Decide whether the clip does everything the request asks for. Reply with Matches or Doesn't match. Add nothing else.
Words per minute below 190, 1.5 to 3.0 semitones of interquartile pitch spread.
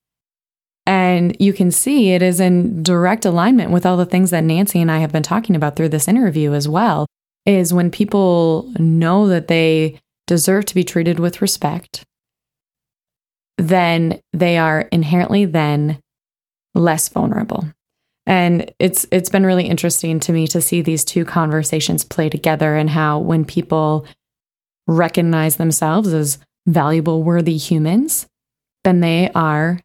Matches